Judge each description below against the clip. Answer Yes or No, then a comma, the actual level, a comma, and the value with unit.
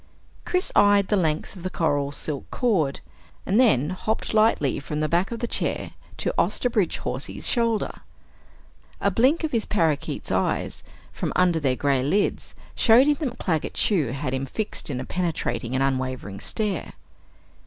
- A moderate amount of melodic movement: No, wide, 7.8 semitones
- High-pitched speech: No, medium, 175 Hz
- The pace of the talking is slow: No, average, 165 wpm